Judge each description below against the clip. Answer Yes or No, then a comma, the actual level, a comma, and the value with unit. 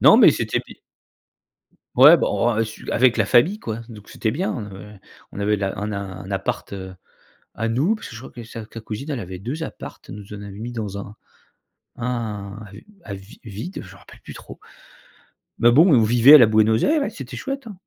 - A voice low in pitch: Yes, low, 110 Hz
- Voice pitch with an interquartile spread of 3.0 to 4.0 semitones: Yes, average, 3.6 semitones